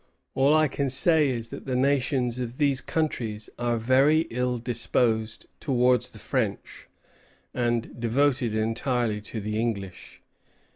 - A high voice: No, low, 125 Hz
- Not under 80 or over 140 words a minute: Yes, slow, 135 wpm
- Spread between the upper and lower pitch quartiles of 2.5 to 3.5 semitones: Yes, average, 2.8 semitones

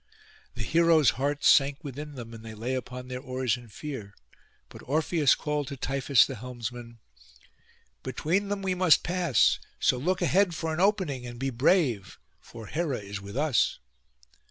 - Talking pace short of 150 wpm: No, average, 165 wpm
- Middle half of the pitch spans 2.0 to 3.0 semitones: No, average, 4.8 semitones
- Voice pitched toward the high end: No, low, 135 Hz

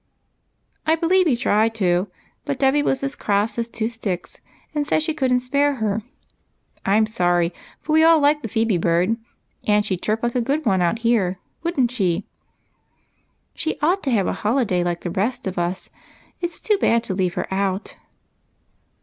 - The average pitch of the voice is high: Yes, high, 225 Hz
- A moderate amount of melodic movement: No, wide, 6.8 semitones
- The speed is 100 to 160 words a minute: No, fast, 205 wpm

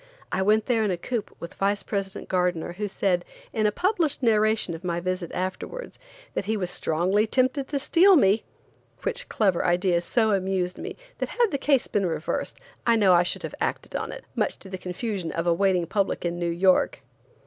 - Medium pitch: No, high, 195 Hz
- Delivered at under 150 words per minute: No, fast, 205 wpm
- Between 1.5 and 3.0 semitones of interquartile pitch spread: No, average, 3.9 semitones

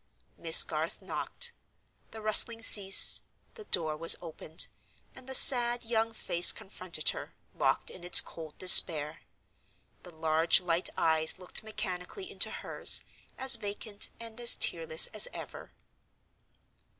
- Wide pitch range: Yes, wide, 5.9 semitones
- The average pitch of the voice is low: No, high, 195 Hz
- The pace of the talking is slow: Yes, slow, 130 wpm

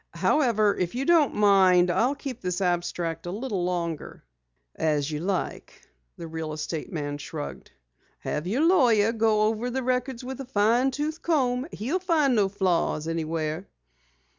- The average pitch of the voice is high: Yes, high, 205 Hz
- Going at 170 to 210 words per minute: No, average, 155 wpm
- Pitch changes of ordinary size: No, wide, 7.0 semitones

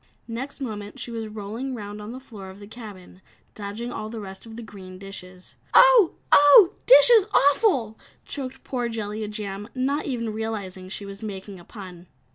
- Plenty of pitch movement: No, average, 4.1 semitones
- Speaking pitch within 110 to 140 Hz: No, high, 215 Hz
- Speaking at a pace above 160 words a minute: Yes, average, 175 wpm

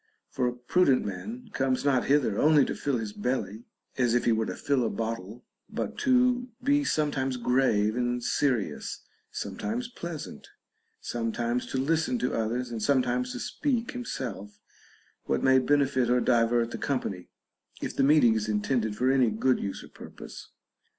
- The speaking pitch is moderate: No, low, 125 Hz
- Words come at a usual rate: Yes, average, 170 wpm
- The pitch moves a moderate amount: Yes, average, 4.0 semitones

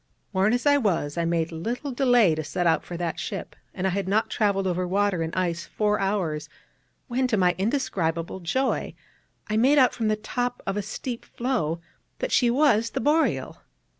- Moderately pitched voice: No, high, 205 Hz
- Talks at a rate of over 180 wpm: Yes, average, 195 wpm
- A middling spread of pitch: No, wide, 5.8 semitones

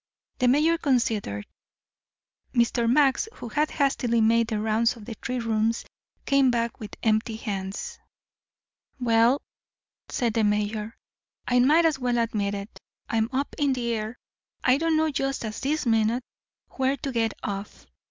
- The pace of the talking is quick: No, average, 150 wpm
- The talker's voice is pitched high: Yes, high, 235 Hz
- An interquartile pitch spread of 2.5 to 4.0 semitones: Yes, average, 3.4 semitones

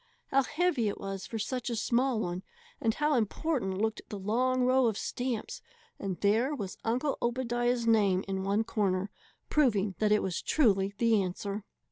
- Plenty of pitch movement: No, average, 4.2 semitones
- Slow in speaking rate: No, average, 170 wpm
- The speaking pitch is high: Yes, high, 225 Hz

